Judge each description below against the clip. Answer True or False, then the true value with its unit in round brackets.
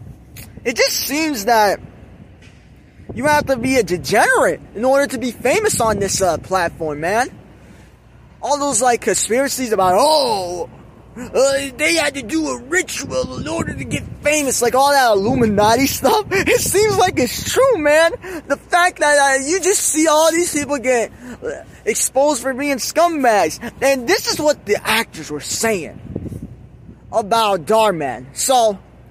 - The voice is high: True (275 Hz)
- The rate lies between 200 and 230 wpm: False (155 wpm)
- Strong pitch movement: True (5.8 semitones)